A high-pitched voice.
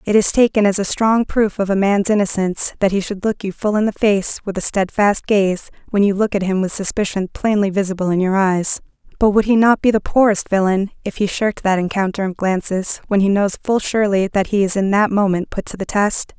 Yes: high, 200 Hz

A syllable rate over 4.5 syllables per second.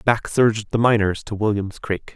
Yes: 4.9 syllables/s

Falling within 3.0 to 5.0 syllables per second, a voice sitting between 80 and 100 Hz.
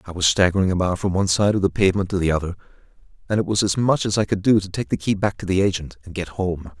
No: 7.0 syllables/s; very low, 95 Hz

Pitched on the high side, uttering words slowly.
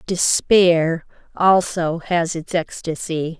No: medium, 170 Hz; slow, 90 wpm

